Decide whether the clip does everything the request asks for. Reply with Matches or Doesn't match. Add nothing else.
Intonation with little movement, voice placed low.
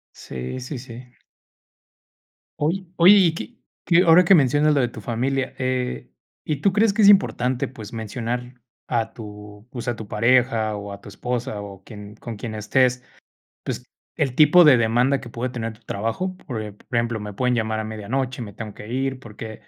Doesn't match